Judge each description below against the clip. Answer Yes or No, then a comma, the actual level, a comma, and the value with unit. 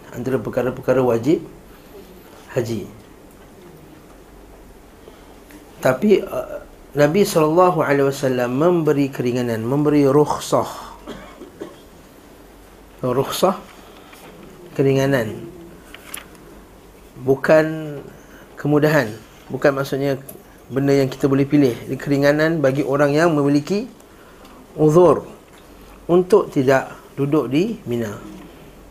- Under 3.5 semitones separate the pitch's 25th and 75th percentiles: Yes, average, 2.7 semitones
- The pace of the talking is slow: Yes, slow, 75 wpm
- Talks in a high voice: No, medium, 140 Hz